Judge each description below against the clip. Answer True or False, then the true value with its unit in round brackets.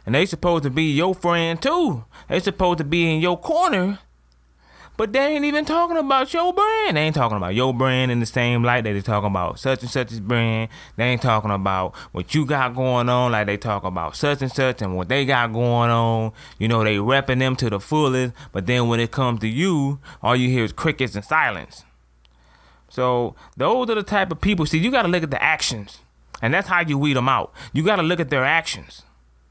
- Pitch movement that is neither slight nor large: False (7.1 semitones)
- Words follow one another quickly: True (230 wpm)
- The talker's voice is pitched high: False (130 Hz)